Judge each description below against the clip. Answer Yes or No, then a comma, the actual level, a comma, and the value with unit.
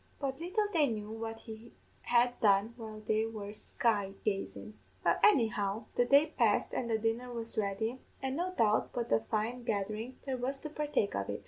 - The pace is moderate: Yes, average, 190 wpm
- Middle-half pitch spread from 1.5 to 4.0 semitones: Yes, average, 2.9 semitones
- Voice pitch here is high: Yes, high, 225 Hz